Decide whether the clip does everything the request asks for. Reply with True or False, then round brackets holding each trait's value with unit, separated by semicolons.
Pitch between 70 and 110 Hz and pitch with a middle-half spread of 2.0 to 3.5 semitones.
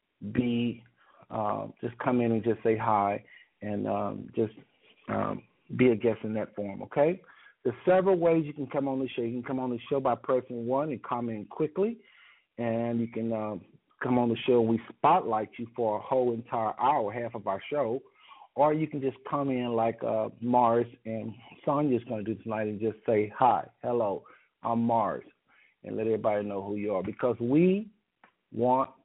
False (120 Hz; 2.9 semitones)